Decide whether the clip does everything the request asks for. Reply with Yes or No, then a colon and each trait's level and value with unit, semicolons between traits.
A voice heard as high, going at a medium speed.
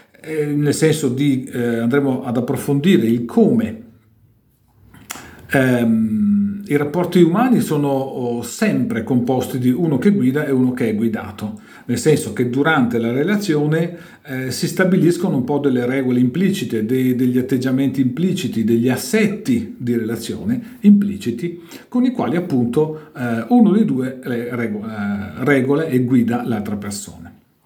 No: low, 135 Hz; average, 135 wpm